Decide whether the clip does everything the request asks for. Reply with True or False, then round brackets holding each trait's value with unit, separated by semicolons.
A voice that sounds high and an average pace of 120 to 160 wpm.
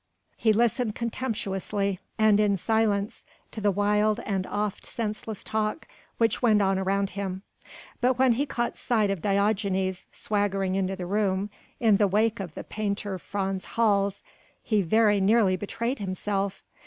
True (205 Hz; 150 wpm)